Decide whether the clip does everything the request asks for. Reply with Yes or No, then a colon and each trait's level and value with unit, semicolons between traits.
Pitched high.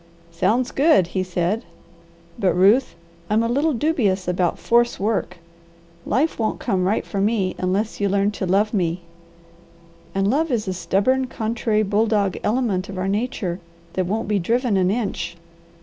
Yes: high, 205 Hz